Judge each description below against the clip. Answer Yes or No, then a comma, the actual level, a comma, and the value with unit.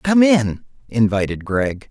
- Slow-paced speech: Yes, slow, 125 wpm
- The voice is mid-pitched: No, low, 125 Hz